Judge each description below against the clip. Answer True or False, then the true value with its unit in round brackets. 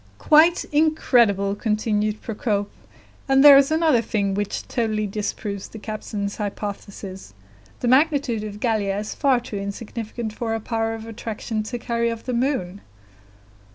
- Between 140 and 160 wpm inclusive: True (145 wpm)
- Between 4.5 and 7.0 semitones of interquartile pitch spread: False (2.9 semitones)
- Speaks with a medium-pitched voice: False (220 Hz)